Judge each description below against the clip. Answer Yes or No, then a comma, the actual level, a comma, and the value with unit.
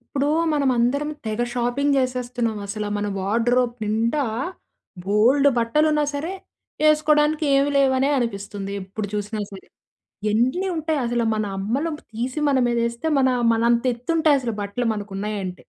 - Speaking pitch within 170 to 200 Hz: No, high, 240 Hz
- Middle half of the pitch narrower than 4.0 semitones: No, average, 4.7 semitones